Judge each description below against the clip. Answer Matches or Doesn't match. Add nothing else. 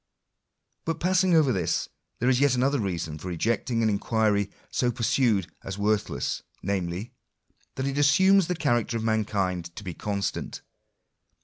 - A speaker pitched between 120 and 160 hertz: Doesn't match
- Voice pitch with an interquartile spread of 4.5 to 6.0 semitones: Matches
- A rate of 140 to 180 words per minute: Matches